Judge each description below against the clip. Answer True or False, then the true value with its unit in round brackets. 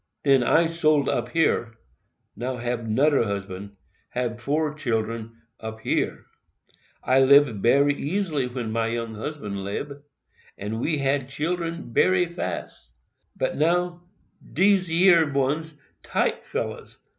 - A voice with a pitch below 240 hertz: True (135 Hz)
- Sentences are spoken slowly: True (115 wpm)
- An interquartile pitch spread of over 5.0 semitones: True (5.4 semitones)